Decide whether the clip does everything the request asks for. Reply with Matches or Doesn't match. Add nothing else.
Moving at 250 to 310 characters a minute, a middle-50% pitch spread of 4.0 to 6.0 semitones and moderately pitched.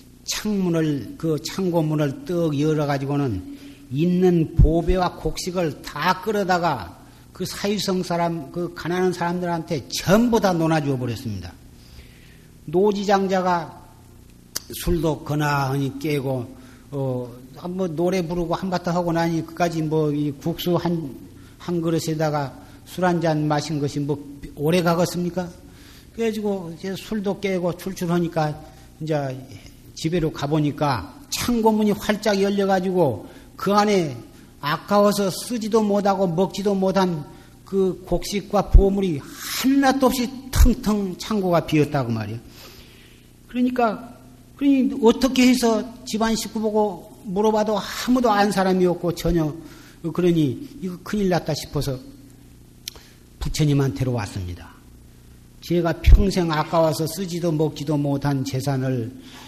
Matches